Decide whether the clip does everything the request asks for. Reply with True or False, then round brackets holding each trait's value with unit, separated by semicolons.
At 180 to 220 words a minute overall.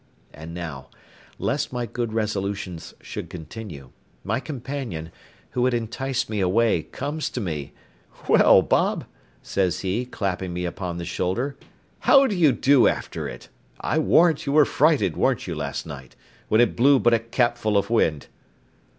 False (160 wpm)